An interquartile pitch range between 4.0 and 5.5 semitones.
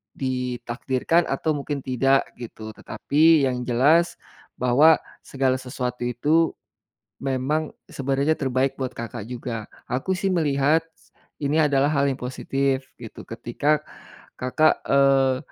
No: average, 2.8 semitones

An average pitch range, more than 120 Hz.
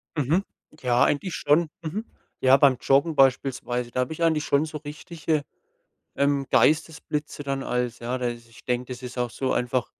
Yes: average, 3.6 semitones; low, 135 Hz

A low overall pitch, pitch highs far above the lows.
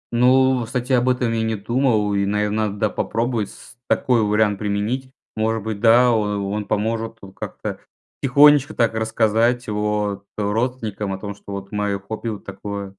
No: low, 110 Hz; average, 2.9 semitones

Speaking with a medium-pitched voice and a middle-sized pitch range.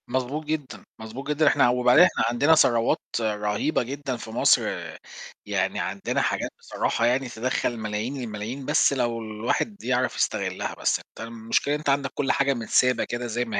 No: low, 125 Hz; average, 3.4 semitones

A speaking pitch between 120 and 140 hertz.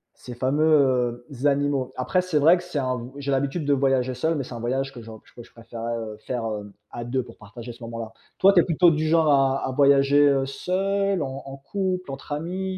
Yes: low, 135 Hz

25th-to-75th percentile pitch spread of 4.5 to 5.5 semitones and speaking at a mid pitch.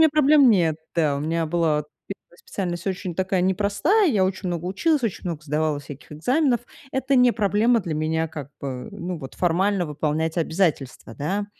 Yes: average, 4.8 semitones; medium, 175 Hz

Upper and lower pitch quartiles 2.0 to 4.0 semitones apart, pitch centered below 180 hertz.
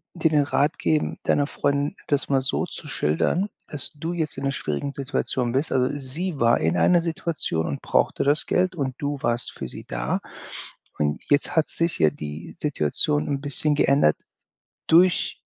No: average, 4.8 semitones; medium, 140 Hz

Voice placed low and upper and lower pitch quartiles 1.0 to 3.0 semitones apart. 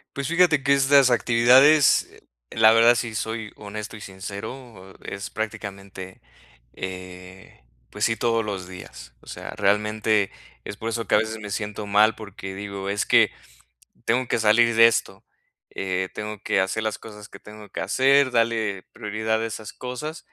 Yes: low, 110 Hz; average, 2.7 semitones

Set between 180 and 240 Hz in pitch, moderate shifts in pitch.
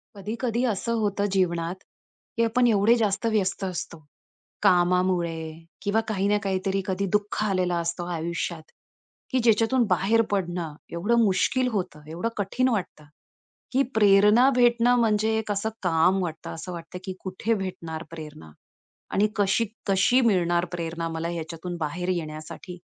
Yes: high, 190 Hz; average, 4.1 semitones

